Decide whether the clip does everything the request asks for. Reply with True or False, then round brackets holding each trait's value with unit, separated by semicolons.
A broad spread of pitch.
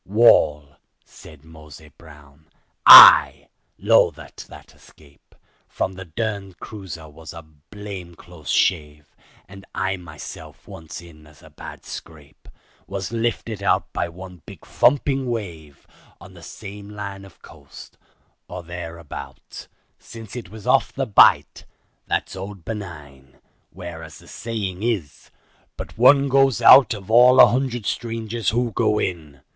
True (5.9 semitones)